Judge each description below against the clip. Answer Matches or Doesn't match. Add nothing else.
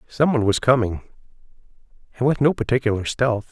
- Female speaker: Doesn't match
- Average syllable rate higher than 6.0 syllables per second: Matches